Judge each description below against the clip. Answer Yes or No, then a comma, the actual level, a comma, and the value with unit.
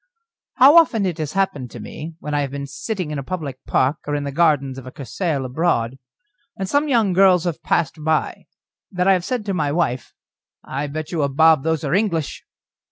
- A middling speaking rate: No, fast, 215 wpm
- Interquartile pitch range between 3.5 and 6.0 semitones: Yes, average, 4.7 semitones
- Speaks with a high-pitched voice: No, medium, 155 Hz